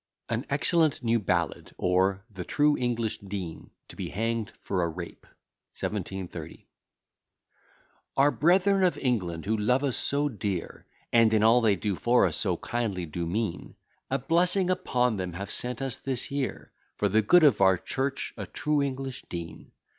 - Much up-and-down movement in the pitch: Yes, wide, 6.2 semitones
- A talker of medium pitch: No, low, 115 Hz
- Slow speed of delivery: No, average, 165 wpm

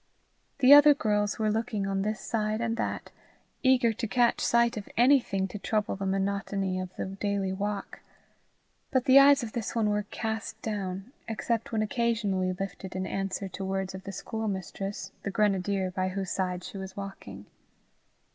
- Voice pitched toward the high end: Yes, high, 205 Hz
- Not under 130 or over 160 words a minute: No, average, 170 wpm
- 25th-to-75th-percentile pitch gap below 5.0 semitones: Yes, average, 2.8 semitones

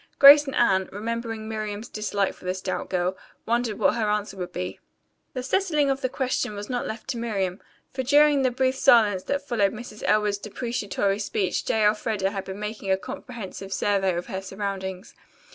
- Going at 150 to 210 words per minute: Yes, average, 185 wpm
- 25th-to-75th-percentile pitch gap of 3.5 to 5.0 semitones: Yes, average, 3.9 semitones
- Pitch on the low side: No, high, 210 Hz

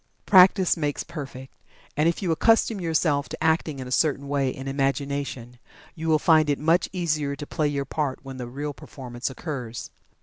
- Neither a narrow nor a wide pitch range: Yes, average, 3.0 semitones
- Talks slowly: No, average, 180 wpm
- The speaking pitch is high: No, medium, 145 Hz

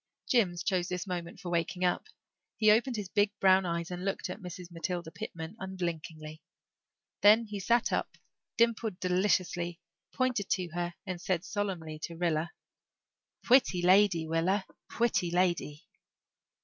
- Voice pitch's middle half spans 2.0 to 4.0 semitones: Yes, average, 3.1 semitones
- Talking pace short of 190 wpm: Yes, average, 140 wpm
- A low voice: No, medium, 180 Hz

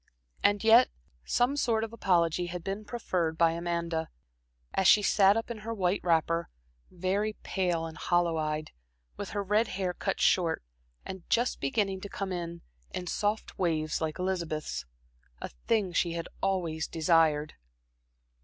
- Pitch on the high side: No, medium, 180 Hz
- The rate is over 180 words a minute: No, average, 155 wpm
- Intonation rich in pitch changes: No, average, 3.6 semitones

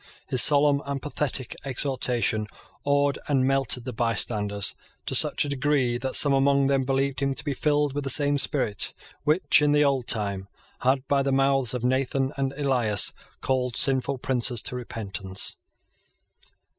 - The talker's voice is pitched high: No, low, 135 Hz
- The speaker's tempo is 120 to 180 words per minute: Yes, average, 160 wpm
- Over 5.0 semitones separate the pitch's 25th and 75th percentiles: No, narrow, 2.4 semitones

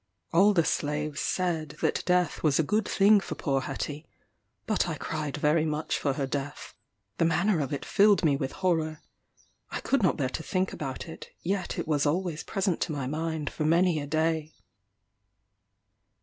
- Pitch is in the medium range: Yes, medium, 160 Hz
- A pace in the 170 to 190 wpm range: Yes, average, 180 wpm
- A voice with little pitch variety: No, average, 3.4 semitones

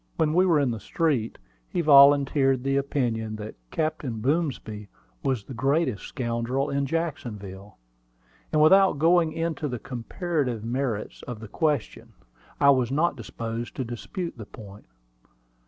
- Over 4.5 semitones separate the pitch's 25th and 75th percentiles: Yes, average, 5.1 semitones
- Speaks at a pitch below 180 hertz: Yes, low, 135 Hz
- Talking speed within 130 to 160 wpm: Yes, average, 140 wpm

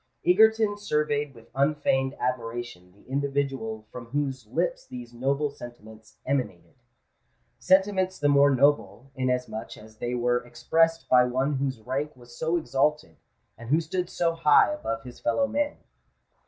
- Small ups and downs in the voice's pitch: No, average, 4.1 semitones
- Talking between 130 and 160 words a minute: Yes, average, 140 wpm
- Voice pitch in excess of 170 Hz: No, low, 135 Hz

